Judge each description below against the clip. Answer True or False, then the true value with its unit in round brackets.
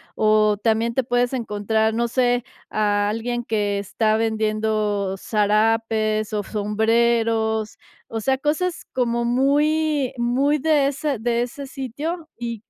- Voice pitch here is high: True (230 Hz)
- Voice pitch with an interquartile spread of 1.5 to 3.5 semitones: True (3.1 semitones)